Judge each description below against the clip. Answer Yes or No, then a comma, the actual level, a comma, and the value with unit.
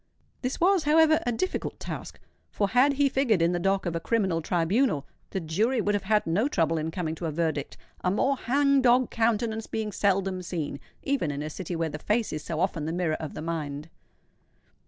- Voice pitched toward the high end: Yes, high, 195 Hz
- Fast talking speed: Yes, fast, 210 wpm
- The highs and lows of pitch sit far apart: Yes, wide, 6.7 semitones